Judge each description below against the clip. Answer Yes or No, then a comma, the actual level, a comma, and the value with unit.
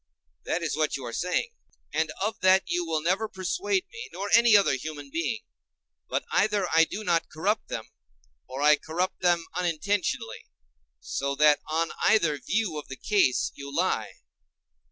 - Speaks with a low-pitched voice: No, medium, 170 Hz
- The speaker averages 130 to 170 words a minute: Yes, average, 165 wpm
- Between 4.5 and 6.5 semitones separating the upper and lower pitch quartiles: Yes, average, 5.2 semitones